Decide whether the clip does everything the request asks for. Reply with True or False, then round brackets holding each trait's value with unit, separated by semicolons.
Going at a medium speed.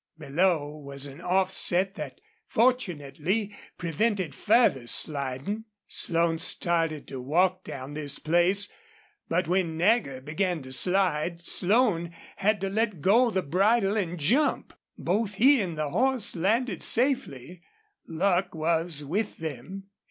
False (125 wpm)